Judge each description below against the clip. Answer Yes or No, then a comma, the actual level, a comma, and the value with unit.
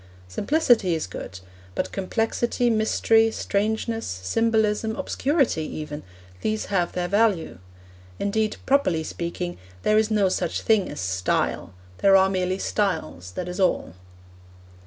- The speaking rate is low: Yes, slow, 125 wpm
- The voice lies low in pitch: No, high, 200 Hz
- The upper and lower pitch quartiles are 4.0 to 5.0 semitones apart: Yes, average, 4.3 semitones